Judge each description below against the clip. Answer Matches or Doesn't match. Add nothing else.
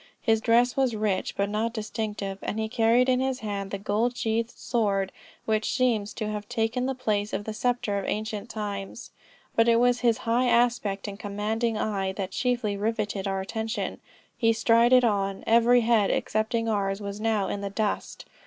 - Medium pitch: Doesn't match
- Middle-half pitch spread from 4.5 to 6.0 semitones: Doesn't match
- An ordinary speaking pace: Matches